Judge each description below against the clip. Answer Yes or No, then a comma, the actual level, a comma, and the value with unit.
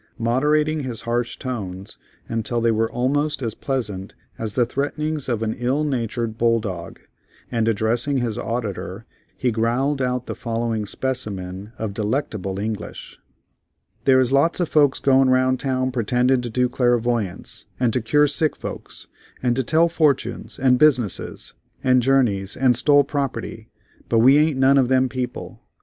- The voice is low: Yes, low, 125 Hz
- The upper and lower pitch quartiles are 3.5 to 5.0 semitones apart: No, average, 3.0 semitones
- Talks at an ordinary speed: Yes, average, 155 wpm